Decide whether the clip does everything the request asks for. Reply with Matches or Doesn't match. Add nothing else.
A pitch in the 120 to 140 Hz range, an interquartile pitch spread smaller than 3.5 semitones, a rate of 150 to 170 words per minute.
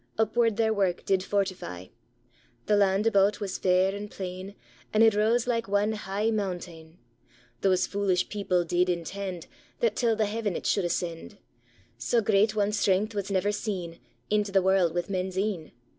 Doesn't match